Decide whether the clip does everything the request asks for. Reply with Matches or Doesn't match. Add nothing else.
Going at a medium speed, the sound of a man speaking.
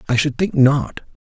Matches